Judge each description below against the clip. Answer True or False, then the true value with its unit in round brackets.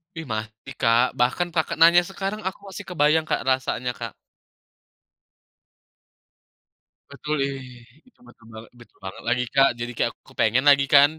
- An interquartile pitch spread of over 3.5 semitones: True (5.3 semitones)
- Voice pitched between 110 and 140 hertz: True (135 Hz)